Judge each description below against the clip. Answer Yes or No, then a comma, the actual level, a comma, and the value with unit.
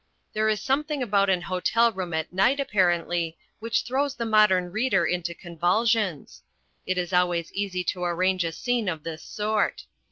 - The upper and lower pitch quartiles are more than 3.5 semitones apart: Yes, average, 4.1 semitones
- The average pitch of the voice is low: No, high, 190 Hz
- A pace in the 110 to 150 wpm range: No, average, 165 wpm